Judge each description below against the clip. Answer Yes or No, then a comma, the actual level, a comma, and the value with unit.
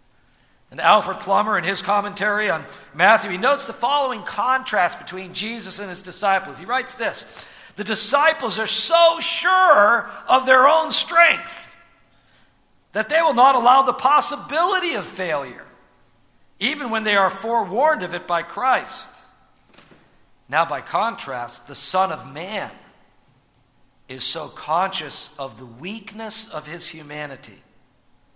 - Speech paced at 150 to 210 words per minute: No, slow, 135 wpm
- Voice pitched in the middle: No, high, 220 Hz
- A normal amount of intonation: No, wide, 6.3 semitones